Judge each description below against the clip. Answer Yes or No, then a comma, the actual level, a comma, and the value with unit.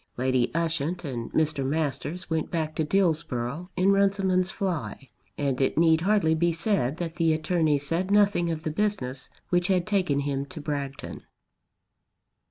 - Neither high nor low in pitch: Yes, medium, 160 Hz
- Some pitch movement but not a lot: Yes, average, 4.3 semitones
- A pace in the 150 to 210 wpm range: Yes, average, 155 wpm